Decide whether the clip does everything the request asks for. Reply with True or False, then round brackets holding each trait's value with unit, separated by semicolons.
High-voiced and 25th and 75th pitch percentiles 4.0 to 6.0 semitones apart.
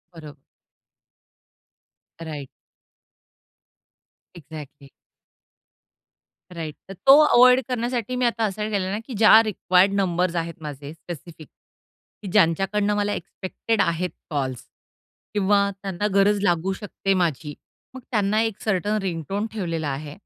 True (195 Hz; 4.3 semitones)